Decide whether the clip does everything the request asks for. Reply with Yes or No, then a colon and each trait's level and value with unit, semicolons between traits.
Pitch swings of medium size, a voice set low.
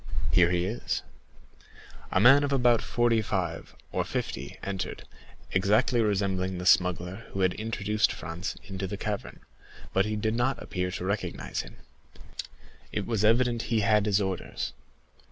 Yes: average, 3.4 semitones; low, 100 Hz